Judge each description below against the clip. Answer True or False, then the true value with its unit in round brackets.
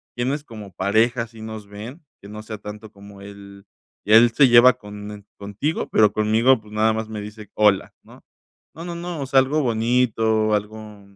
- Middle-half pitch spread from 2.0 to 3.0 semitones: True (2.7 semitones)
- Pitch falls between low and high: False (110 Hz)